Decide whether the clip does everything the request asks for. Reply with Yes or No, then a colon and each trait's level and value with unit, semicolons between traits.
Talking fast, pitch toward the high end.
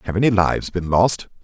No: fast, 210 wpm; low, 100 Hz